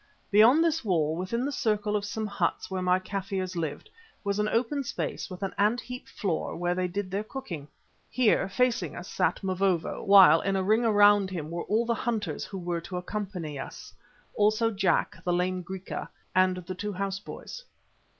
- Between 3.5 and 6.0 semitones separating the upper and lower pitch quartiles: No, average, 2.9 semitones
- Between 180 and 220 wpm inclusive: Yes, average, 190 wpm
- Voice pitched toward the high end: Yes, high, 195 Hz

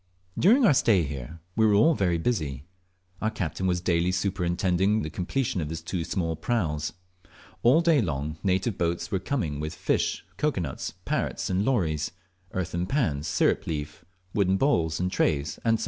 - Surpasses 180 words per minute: No, average, 170 wpm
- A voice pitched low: Yes, very low, 90 Hz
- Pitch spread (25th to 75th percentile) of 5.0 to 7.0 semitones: Yes, wide, 5.4 semitones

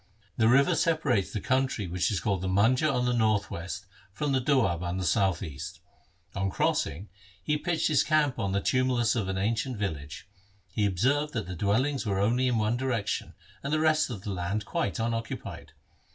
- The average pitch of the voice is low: Yes, low, 110 Hz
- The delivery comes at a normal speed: Yes, average, 195 wpm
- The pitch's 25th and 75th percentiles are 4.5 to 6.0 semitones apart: Yes, average, 5.1 semitones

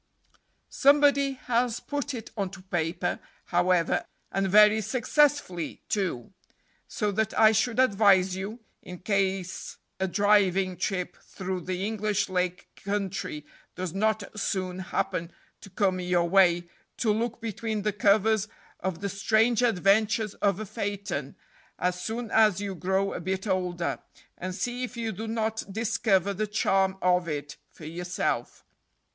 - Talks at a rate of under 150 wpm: Yes, average, 140 wpm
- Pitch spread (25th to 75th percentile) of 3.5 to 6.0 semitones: No, average, 3.1 semitones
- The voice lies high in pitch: Yes, high, 195 Hz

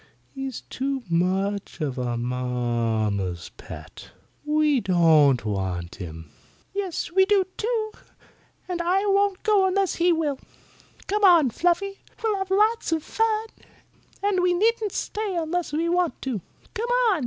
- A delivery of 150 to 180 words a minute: No, average, 140 wpm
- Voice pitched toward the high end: Yes, very high, 325 Hz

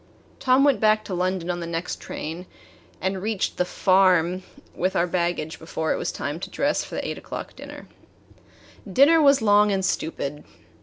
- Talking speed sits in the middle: Yes, average, 185 wpm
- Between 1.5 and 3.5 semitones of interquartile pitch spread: No, average, 3.9 semitones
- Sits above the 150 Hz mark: Yes, medium, 185 Hz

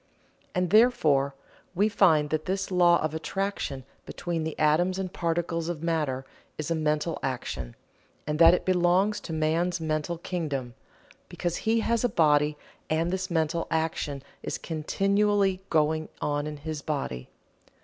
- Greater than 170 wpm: No, average, 150 wpm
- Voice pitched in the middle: Yes, medium, 165 Hz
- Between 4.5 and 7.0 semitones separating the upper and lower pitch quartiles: No, average, 3.1 semitones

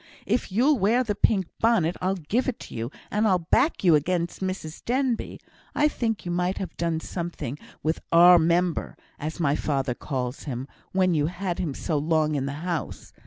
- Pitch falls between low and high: Yes, medium, 175 Hz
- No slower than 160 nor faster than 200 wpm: Yes, average, 185 wpm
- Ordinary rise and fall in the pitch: Yes, average, 4.1 semitones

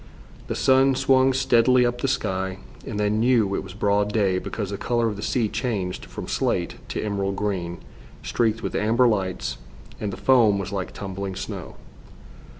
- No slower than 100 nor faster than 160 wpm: No, average, 175 wpm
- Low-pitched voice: Yes, low, 105 Hz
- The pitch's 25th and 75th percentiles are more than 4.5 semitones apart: No, average, 3.6 semitones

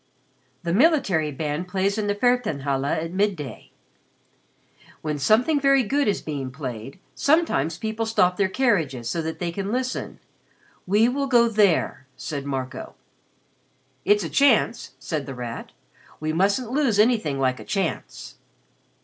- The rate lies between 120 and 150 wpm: Yes, average, 145 wpm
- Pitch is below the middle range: No, high, 190 Hz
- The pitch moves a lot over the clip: Yes, wide, 7.8 semitones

